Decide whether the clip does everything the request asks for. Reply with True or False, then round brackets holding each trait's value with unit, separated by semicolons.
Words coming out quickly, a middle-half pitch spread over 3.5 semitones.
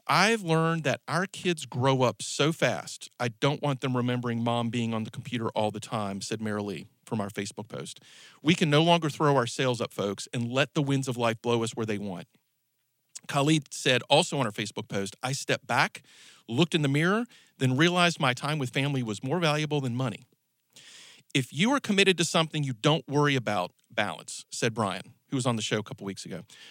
True (215 wpm; 4.6 semitones)